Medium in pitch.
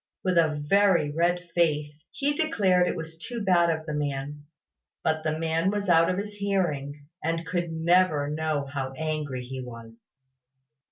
Yes: medium, 160 Hz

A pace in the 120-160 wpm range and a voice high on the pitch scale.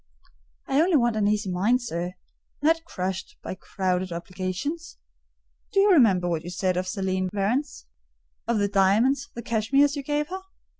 Yes: average, 155 wpm; high, 210 Hz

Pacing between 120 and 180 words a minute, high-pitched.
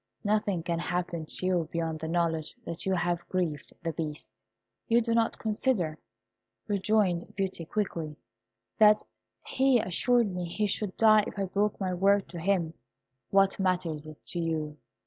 No: average, 160 wpm; medium, 180 Hz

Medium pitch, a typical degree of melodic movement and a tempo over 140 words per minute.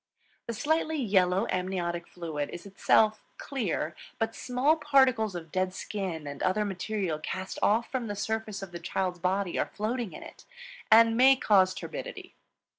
No: high, 200 Hz; average, 4.2 semitones; average, 160 wpm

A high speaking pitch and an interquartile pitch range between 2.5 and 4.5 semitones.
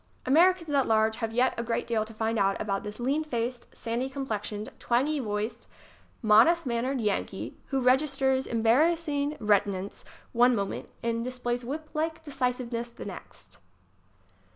Yes: high, 240 Hz; average, 3.8 semitones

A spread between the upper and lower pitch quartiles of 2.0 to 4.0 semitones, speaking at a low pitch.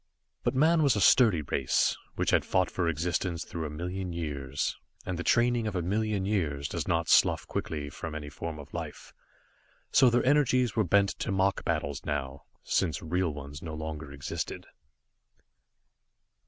No: average, 5.3 semitones; very low, 85 Hz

